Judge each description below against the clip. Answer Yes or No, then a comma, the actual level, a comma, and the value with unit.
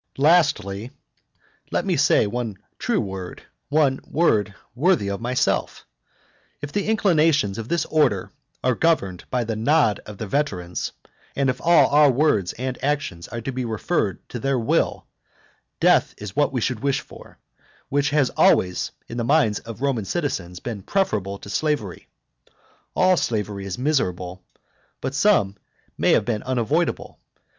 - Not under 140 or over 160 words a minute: Yes, average, 155 wpm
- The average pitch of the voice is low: Yes, low, 125 Hz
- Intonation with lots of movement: Yes, wide, 6.3 semitones